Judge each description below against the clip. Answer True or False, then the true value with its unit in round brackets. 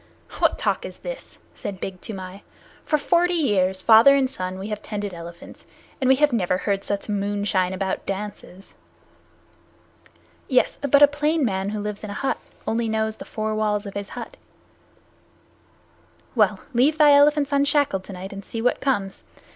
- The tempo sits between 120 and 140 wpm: False (165 wpm)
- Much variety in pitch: True (6.1 semitones)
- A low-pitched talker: False (210 Hz)